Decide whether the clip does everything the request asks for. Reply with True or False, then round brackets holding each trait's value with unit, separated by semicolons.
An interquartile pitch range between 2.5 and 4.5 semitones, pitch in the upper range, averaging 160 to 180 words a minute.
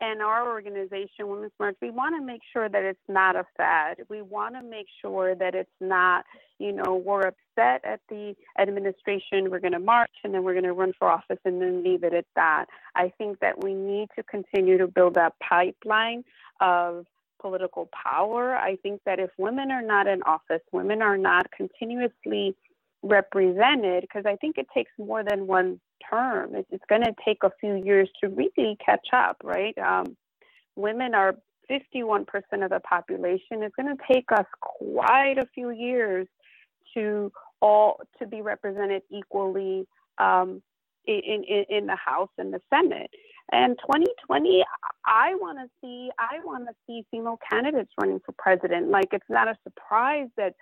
True (4.0 semitones; 205 Hz; 175 wpm)